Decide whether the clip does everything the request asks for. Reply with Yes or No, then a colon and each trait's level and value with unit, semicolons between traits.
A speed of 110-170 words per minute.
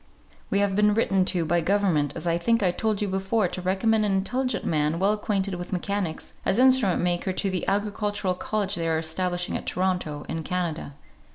No: average, 195 wpm